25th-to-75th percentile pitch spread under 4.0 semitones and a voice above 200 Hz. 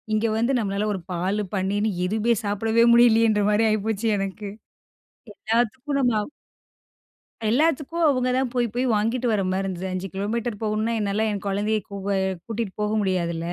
Yes: average, 2.9 semitones; high, 215 Hz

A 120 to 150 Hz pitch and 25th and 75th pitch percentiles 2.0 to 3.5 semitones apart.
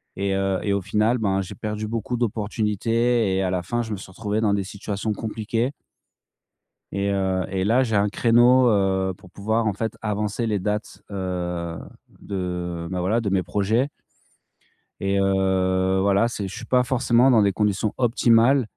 No: low, 105 Hz; average, 3.0 semitones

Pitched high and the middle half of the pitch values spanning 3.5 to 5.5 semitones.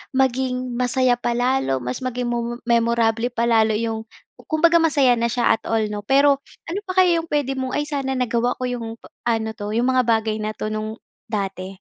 No: high, 240 Hz; average, 2.8 semitones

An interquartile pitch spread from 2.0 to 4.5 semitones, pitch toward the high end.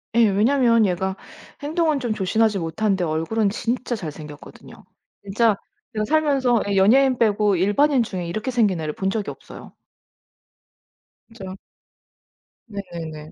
Yes: average, 4.1 semitones; high, 210 Hz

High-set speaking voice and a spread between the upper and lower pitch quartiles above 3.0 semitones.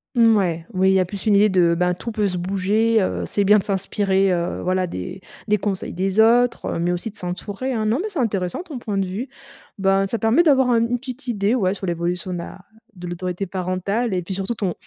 Yes: high, 195 Hz; average, 3.5 semitones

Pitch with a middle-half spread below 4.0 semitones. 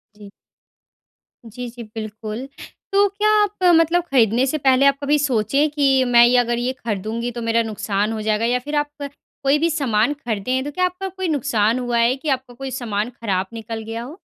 No: average, 4.3 semitones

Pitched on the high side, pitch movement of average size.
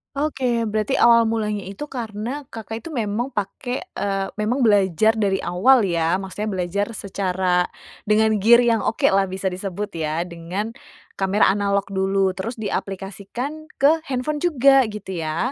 Yes: high, 205 Hz; average, 3.6 semitones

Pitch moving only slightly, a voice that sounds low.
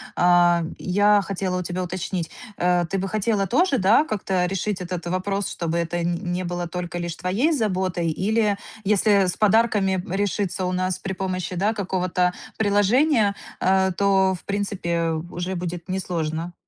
No: narrow, 2.3 semitones; medium, 185 Hz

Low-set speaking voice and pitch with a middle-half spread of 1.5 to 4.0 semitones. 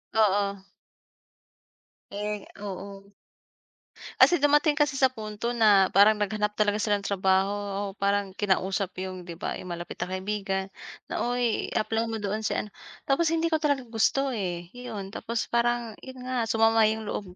No: high, 210 Hz; average, 3.3 semitones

